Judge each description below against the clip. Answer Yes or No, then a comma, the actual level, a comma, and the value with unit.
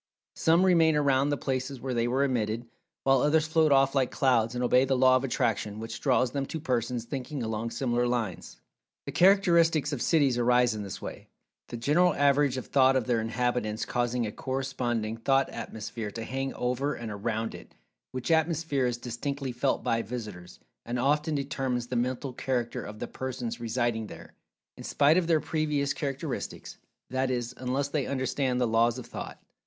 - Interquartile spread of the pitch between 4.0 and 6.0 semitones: No, average, 2.9 semitones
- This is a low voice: Yes, low, 130 Hz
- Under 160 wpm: No, average, 180 wpm